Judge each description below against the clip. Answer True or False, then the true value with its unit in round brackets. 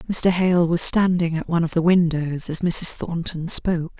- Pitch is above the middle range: False (170 Hz)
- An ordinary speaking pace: True (195 wpm)